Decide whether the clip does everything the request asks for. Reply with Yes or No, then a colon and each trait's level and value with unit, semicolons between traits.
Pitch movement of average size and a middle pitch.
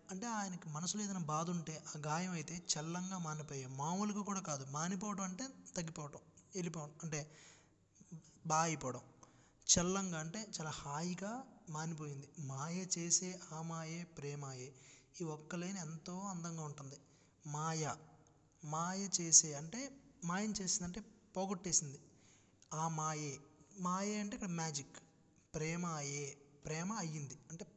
Yes: average, 3.5 semitones; medium, 160 Hz